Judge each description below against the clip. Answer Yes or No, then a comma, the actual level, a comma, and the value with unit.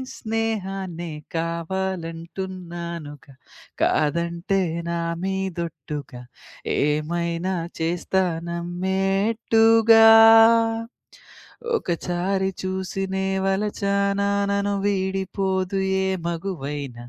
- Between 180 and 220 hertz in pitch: Yes, high, 190 Hz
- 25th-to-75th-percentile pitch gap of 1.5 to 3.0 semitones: Yes, narrow, 2.4 semitones